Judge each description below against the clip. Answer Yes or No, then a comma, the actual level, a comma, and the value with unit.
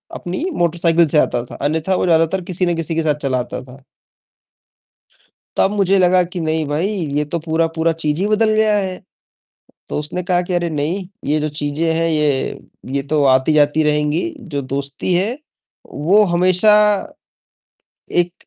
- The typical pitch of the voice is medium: Yes, medium, 165 Hz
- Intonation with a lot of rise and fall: No, average, 3.3 semitones